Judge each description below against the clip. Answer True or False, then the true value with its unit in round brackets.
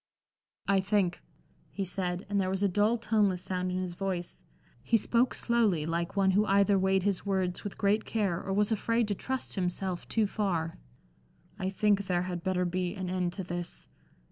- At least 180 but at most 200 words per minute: True (190 wpm)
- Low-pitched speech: False (190 Hz)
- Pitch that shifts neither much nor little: False (2.3 semitones)